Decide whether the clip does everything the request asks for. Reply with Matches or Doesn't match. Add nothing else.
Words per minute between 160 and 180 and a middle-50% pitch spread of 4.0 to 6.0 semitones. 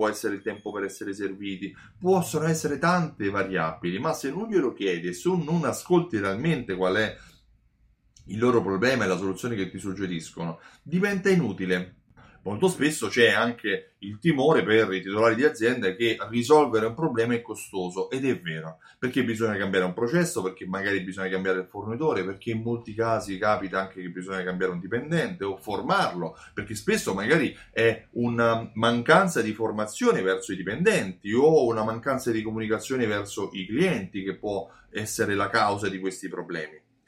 Matches